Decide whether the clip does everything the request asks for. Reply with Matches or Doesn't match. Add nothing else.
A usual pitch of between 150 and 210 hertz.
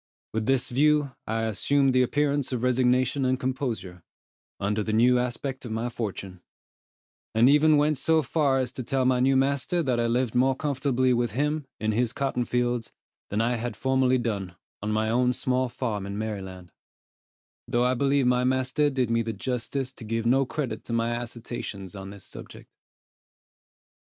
Doesn't match